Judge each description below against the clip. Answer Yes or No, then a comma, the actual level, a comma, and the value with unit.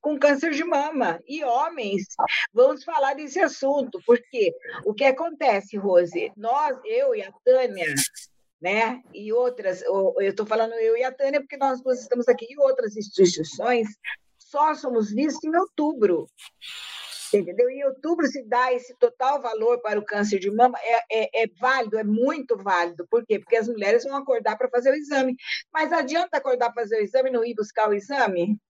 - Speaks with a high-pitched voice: Yes, very high, 255 Hz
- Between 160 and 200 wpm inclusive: Yes, fast, 185 wpm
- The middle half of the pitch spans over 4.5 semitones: Yes, average, 5.1 semitones